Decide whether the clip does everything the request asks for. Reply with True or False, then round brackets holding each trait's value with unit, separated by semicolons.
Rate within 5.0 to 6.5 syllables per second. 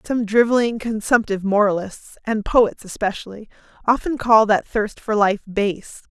False (4.6 syllables/s)